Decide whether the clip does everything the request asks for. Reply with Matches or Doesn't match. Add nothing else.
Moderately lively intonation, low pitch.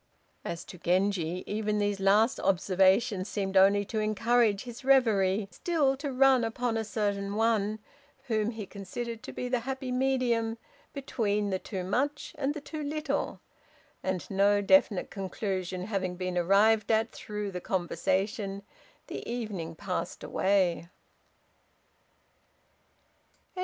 Doesn't match